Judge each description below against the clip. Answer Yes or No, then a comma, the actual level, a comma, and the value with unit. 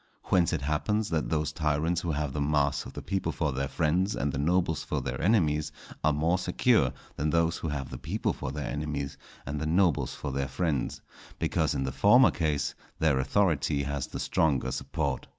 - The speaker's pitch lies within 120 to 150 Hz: No, very low, 75 Hz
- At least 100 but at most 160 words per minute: No, average, 200 wpm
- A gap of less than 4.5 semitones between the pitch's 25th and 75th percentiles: Yes, average, 3.1 semitones